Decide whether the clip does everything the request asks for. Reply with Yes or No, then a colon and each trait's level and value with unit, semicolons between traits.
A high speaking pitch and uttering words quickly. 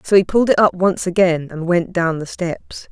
No: medium, 180 Hz; fast, 245 wpm